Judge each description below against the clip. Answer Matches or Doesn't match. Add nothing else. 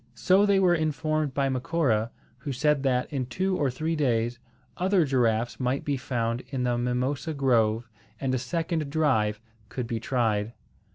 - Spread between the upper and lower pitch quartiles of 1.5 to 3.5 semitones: Doesn't match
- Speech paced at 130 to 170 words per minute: Matches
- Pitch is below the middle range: Matches